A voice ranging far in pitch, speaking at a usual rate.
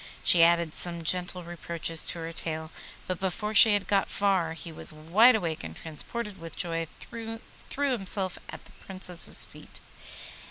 No: average, 3.4 semitones; average, 160 wpm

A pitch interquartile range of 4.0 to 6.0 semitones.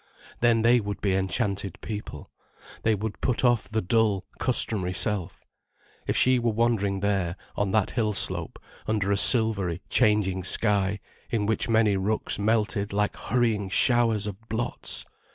No: narrow, 2.5 semitones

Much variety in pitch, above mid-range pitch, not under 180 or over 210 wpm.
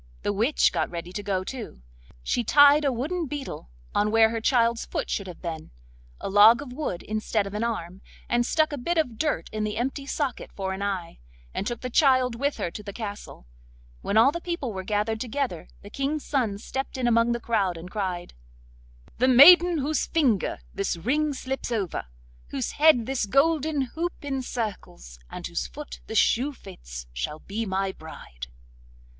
Yes: wide, 6.0 semitones; high, 230 Hz; average, 185 wpm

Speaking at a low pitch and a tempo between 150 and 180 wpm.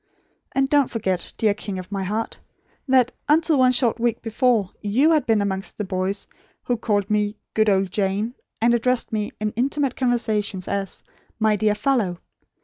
No: high, 215 Hz; average, 170 wpm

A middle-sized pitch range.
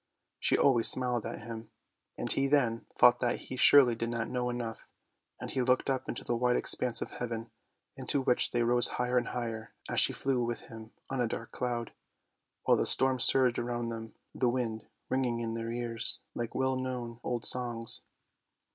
No: narrow, 1.5 semitones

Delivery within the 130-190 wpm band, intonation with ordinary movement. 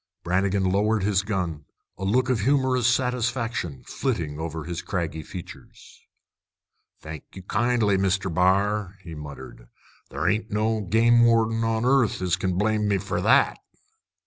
Yes: average, 145 wpm; average, 3.9 semitones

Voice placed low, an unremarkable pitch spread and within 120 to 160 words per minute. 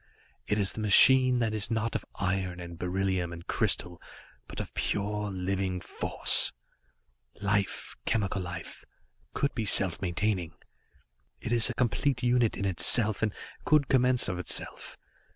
Yes: low, 100 Hz; average, 4.1 semitones; average, 145 wpm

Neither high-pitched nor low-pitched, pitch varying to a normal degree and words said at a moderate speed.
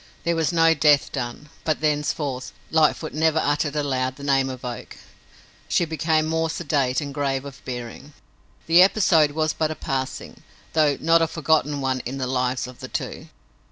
Yes: medium, 145 Hz; average, 3.2 semitones; average, 175 wpm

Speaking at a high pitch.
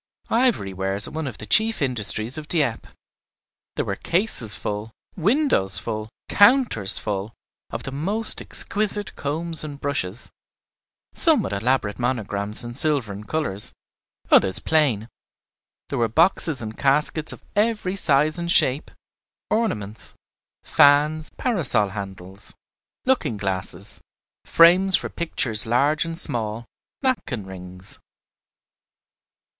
No: low, 135 Hz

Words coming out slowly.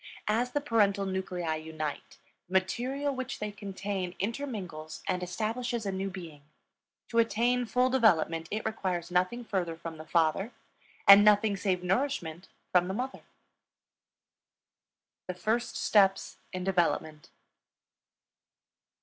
Yes: slow, 125 wpm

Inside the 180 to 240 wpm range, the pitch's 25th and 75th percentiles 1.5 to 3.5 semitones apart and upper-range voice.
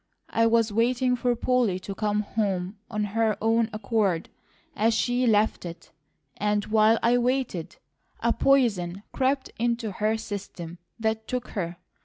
No: average, 145 wpm; average, 2.7 semitones; high, 220 Hz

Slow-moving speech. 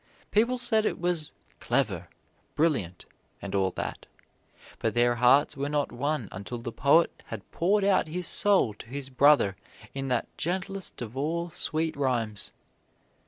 No: average, 150 wpm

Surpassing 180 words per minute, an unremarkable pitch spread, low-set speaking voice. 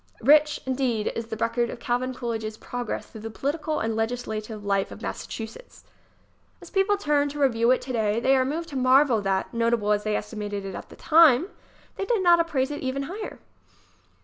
No: average, 195 wpm; average, 4.8 semitones; high, 245 Hz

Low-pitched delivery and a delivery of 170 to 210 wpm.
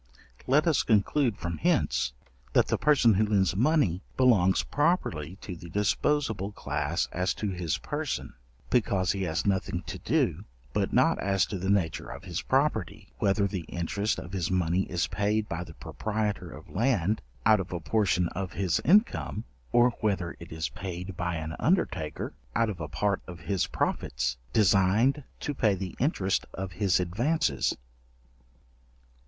No: very low, 95 Hz; average, 160 wpm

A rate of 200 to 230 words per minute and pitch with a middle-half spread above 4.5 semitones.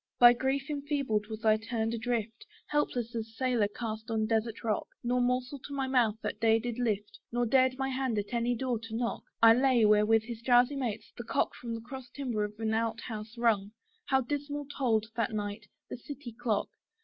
No: fast, 205 wpm; narrow, 2.6 semitones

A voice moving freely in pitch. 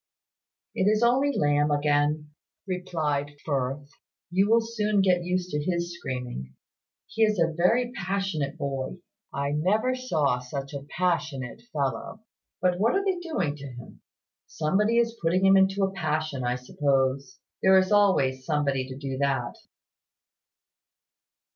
Yes: wide, 5.7 semitones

